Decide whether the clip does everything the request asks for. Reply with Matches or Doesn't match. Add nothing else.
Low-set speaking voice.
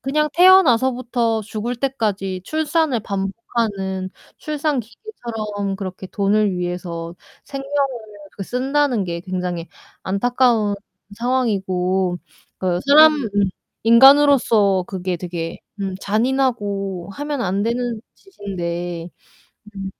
Doesn't match